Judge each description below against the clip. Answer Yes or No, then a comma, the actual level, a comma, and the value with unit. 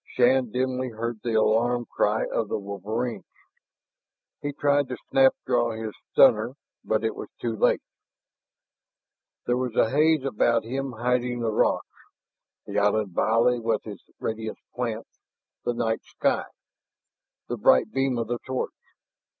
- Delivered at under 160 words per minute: Yes, average, 140 wpm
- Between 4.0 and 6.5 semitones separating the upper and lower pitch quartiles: No, narrow, 2.4 semitones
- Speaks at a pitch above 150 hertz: No, low, 120 Hz